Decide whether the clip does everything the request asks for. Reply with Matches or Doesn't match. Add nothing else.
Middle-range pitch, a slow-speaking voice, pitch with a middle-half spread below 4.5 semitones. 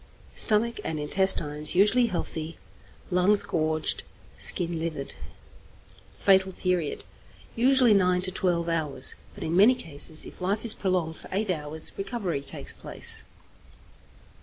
Matches